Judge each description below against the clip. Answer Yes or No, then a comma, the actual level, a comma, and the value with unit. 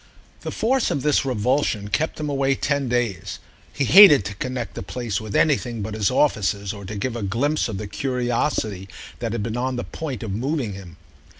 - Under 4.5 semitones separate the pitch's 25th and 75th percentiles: No, average, 5.1 semitones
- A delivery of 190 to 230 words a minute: Yes, average, 200 wpm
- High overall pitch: No, low, 120 Hz